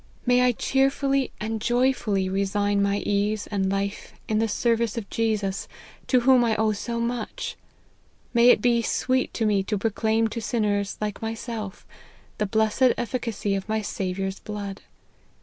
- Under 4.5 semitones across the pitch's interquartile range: Yes, average, 2.7 semitones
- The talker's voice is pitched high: Yes, high, 220 Hz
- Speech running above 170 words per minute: No, average, 155 wpm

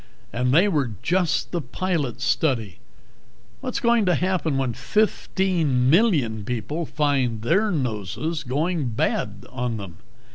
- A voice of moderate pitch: Yes, medium, 145 Hz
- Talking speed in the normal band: No, slow, 130 wpm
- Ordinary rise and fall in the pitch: No, wide, 6.6 semitones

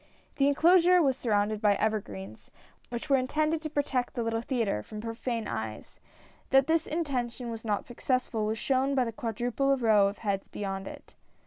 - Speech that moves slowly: No, average, 175 wpm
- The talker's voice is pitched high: Yes, high, 235 Hz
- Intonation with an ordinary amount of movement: Yes, average, 4.4 semitones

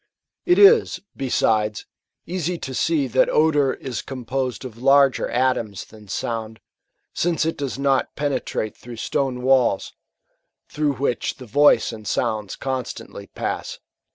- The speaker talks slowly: Yes, slow, 130 wpm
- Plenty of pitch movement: No, average, 3.6 semitones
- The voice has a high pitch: No, low, 130 Hz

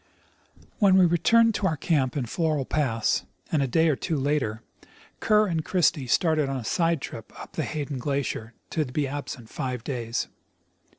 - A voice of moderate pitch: Yes, medium, 145 Hz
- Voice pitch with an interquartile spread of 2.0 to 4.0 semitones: No, average, 4.5 semitones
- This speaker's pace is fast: No, average, 175 wpm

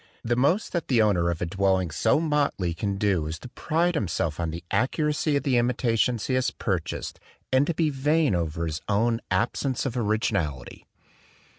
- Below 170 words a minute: No, average, 180 wpm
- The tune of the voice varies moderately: No, wide, 7.7 semitones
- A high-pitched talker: No, low, 115 Hz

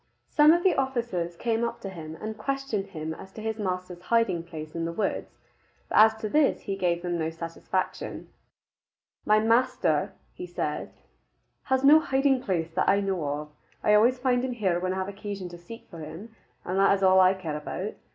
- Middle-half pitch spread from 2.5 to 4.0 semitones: No, average, 5.0 semitones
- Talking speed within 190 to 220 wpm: Yes, average, 200 wpm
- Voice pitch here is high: Yes, high, 195 Hz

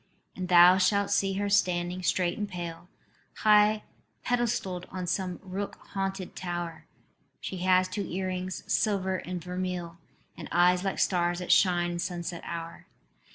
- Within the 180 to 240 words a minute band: No, average, 145 wpm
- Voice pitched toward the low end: No, medium, 185 Hz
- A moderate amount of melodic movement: No, narrow, 1.7 semitones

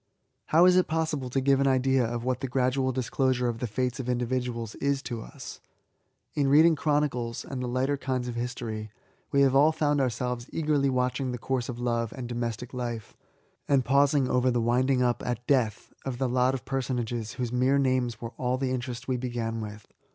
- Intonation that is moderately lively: No, narrow, 2.0 semitones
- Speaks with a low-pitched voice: Yes, low, 125 Hz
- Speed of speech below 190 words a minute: No, average, 200 wpm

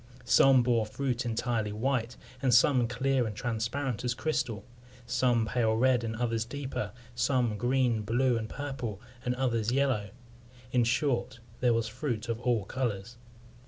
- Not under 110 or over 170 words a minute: Yes, average, 150 wpm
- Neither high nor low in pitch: No, low, 120 Hz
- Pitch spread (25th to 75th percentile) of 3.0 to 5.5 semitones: No, narrow, 2.5 semitones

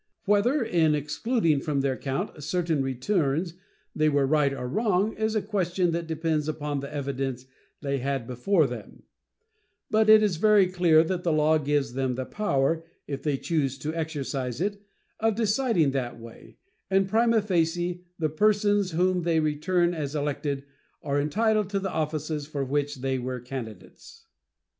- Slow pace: No, average, 160 wpm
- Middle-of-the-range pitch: Yes, medium, 155 Hz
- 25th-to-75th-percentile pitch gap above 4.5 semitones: Yes, average, 5.2 semitones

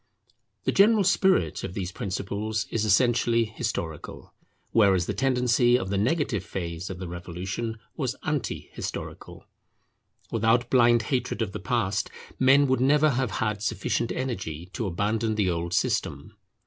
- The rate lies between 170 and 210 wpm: No, average, 145 wpm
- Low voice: Yes, low, 110 Hz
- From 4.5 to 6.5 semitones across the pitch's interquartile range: Yes, average, 5.0 semitones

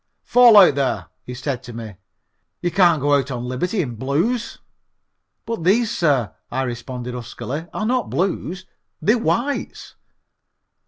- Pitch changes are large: Yes, wide, 8.5 semitones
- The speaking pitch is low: No, medium, 145 Hz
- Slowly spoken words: No, average, 145 wpm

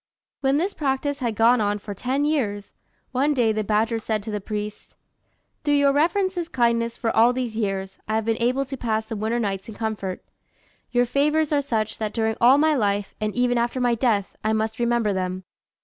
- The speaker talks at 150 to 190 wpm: No, fast, 205 wpm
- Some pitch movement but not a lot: Yes, average, 3.7 semitones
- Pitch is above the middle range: Yes, high, 230 Hz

